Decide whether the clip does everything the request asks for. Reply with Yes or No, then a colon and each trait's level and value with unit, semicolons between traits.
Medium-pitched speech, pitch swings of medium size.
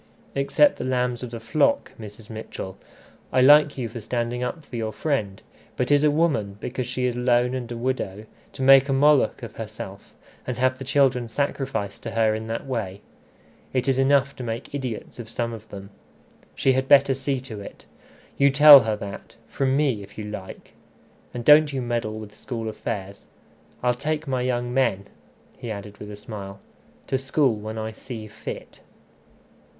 No: low, 125 Hz; average, 3.6 semitones